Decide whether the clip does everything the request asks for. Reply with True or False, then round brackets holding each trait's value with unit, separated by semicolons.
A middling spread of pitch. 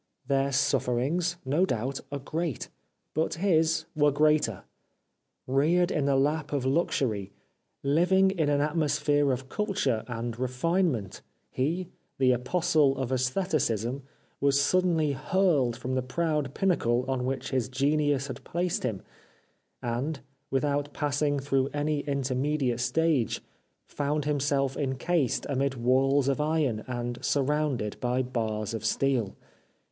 True (3.1 semitones)